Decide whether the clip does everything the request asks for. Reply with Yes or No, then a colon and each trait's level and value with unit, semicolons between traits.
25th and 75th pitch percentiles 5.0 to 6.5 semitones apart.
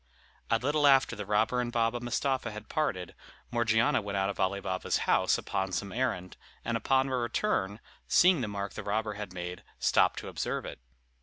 No: average, 3.9 semitones